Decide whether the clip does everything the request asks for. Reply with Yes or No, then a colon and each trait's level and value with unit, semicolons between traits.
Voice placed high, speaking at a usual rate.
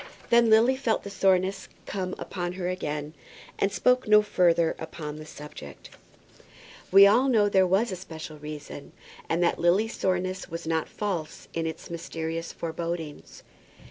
No: medium, 180 Hz; average, 155 wpm